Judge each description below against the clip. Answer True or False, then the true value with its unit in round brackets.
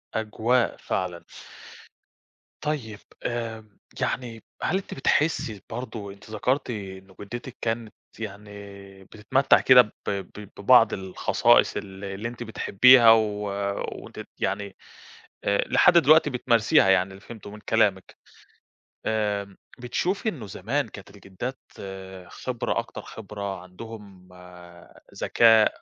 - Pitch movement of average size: True (3.5 semitones)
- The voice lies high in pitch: False (110 Hz)